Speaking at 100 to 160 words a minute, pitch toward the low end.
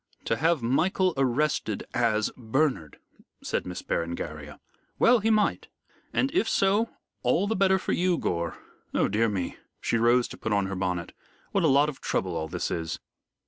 No: average, 175 wpm; low, 120 Hz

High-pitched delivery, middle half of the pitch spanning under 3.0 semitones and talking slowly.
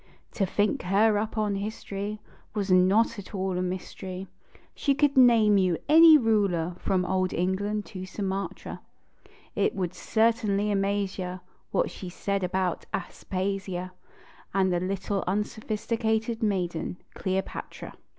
Yes: high, 195 Hz; narrow, 2.5 semitones; slow, 130 wpm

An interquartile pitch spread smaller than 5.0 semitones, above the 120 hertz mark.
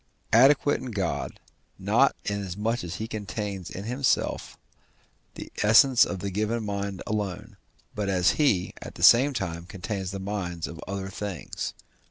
No: average, 2.9 semitones; low, 100 Hz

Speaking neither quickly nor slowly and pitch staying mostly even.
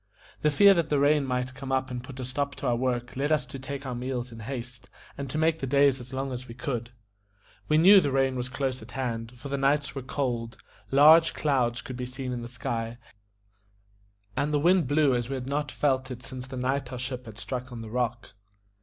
No: fast, 235 wpm; narrow, 2.2 semitones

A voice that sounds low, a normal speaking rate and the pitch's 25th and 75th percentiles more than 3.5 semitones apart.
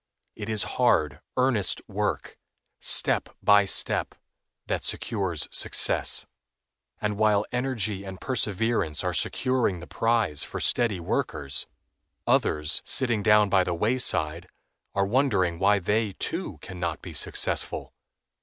No: low, 105 Hz; slow, 125 wpm; average, 4.1 semitones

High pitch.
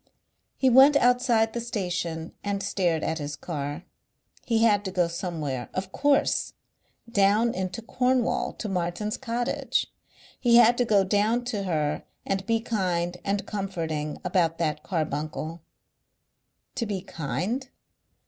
Yes: high, 195 Hz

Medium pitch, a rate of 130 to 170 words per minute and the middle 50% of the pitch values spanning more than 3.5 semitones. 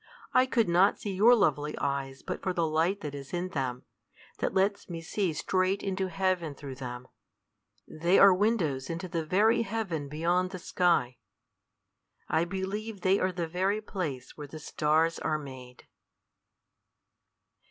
Yes: medium, 175 Hz; average, 155 wpm; average, 4.4 semitones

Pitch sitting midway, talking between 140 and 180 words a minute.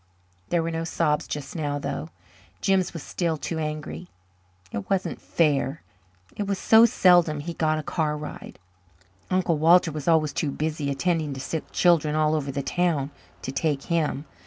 Yes: medium, 155 Hz; average, 170 wpm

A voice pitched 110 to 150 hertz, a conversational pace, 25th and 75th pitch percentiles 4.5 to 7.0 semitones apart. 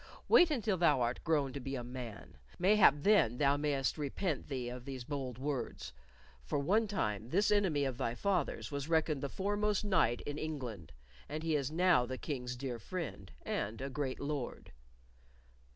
Yes: medium, 140 Hz; average, 175 wpm; average, 5.1 semitones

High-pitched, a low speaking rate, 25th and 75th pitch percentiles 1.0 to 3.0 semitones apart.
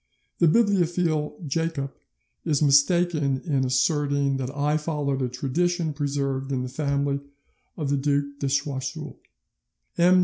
No: medium, 145 Hz; slow, 130 wpm; average, 2.7 semitones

